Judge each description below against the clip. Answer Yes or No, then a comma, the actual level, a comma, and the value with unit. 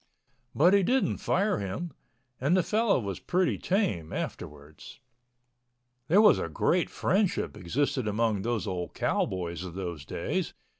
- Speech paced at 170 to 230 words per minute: No, average, 140 wpm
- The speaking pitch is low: Yes, low, 115 Hz